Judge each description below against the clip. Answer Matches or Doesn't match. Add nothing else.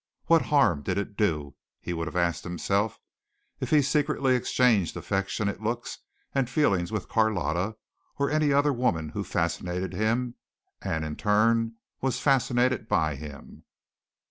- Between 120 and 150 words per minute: Matches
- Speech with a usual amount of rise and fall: Doesn't match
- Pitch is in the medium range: Doesn't match